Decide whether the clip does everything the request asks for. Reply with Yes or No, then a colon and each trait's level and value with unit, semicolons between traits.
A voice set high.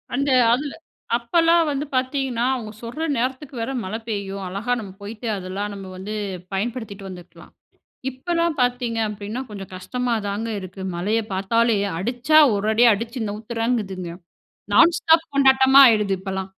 Yes: high, 230 Hz